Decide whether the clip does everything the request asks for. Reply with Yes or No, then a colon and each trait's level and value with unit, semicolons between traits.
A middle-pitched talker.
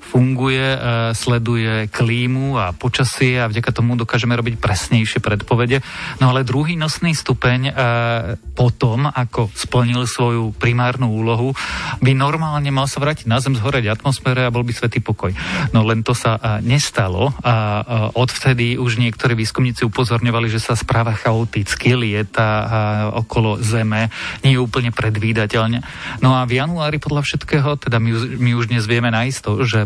No: low, 120 Hz